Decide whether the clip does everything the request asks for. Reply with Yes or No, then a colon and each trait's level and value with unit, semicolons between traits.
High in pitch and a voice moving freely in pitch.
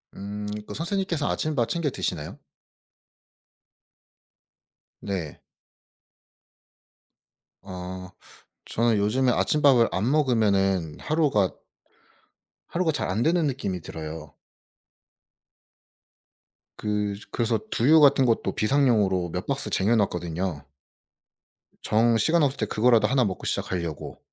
No: low, 110 Hz; wide, 6.4 semitones